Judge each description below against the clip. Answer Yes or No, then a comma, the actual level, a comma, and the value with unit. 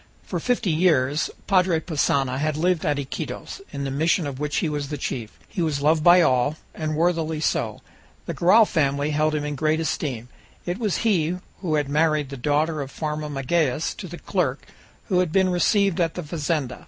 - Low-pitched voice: No, medium, 155 Hz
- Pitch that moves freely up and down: No, average, 3.3 semitones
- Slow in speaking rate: No, average, 195 wpm